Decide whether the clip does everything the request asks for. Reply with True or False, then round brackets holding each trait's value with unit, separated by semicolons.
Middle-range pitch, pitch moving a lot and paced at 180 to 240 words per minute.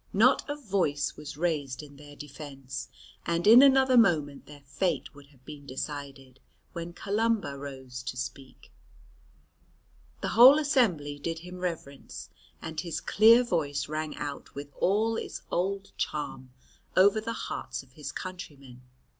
False (155 Hz; 6.0 semitones; 145 wpm)